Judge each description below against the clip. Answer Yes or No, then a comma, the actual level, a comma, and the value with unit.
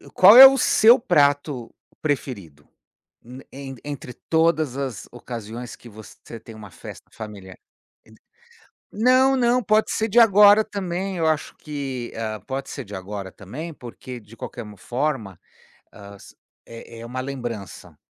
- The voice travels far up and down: Yes, wide, 7.7 semitones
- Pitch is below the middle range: Yes, low, 130 Hz